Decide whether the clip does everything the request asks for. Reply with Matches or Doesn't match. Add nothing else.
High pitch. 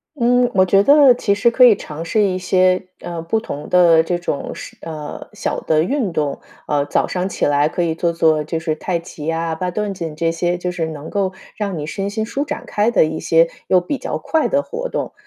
Doesn't match